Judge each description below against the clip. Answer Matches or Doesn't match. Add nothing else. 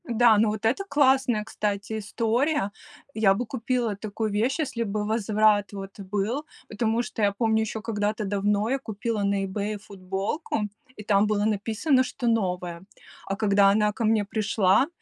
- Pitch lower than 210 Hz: Doesn't match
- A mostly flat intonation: Matches